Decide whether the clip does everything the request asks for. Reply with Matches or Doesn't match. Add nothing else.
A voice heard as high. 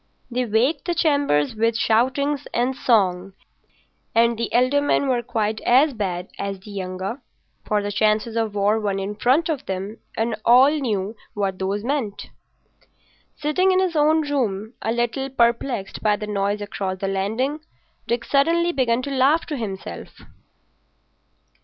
Matches